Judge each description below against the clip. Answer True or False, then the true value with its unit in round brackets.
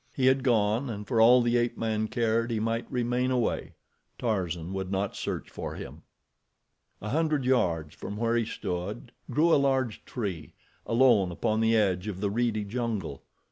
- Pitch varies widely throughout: False (3.4 semitones)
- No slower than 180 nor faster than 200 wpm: False (170 wpm)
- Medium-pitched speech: False (115 Hz)